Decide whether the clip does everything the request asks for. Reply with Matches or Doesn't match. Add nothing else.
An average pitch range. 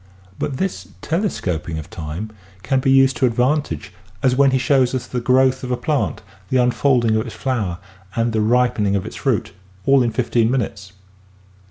Matches